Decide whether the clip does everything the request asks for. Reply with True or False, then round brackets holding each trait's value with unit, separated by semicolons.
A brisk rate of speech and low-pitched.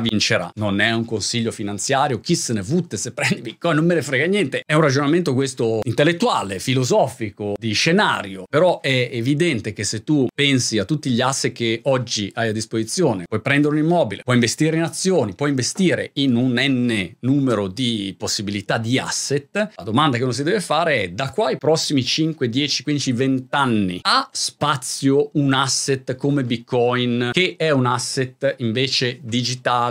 True (180 wpm; 130 Hz)